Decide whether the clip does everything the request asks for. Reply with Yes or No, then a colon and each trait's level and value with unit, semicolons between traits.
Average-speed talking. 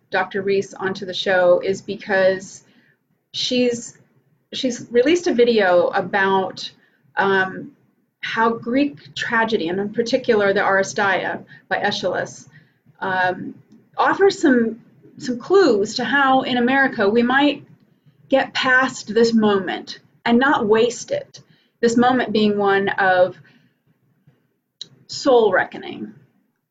No: slow, 110 wpm